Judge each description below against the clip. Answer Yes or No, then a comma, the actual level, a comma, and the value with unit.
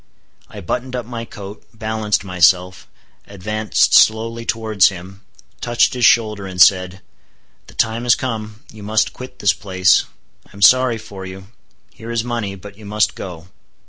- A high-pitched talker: No, low, 105 Hz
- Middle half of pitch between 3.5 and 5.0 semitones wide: No, average, 3.0 semitones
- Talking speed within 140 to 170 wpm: Yes, average, 160 wpm